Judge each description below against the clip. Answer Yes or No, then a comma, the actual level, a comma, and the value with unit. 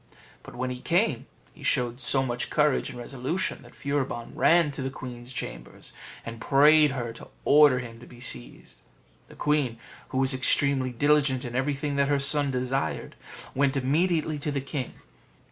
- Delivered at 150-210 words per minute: Yes, average, 170 wpm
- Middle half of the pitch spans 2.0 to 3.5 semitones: Yes, average, 2.8 semitones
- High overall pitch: No, low, 135 Hz